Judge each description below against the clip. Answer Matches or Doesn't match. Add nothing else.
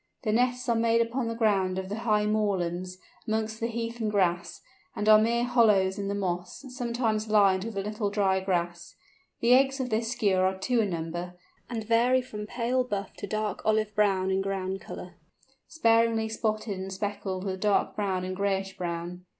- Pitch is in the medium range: Doesn't match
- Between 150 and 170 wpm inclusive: Doesn't match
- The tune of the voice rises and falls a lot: Doesn't match